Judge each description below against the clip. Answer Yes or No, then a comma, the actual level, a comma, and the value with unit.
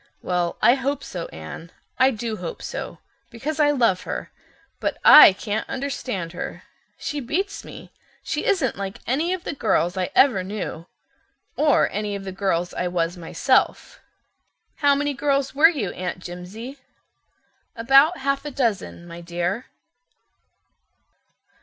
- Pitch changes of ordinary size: No, wide, 7.5 semitones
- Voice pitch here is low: No, high, 230 Hz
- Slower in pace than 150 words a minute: Yes, average, 140 wpm